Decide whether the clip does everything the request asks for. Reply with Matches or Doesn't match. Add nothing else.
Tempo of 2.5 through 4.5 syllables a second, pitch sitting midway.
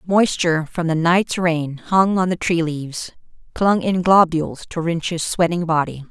Matches